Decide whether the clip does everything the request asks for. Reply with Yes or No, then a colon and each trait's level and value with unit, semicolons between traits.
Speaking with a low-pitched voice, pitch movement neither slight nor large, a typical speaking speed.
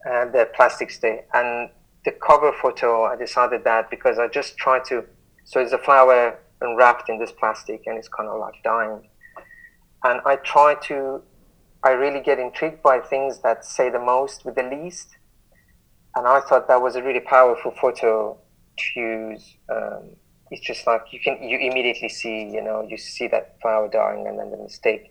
Yes: low, 125 Hz; average, 3.1 semitones; average, 190 wpm